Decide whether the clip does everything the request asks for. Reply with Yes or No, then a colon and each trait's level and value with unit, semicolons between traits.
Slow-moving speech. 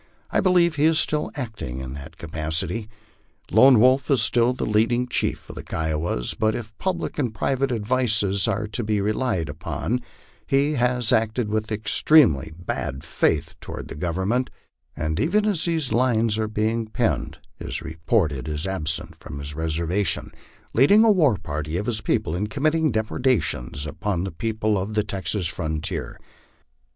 No: average, 160 wpm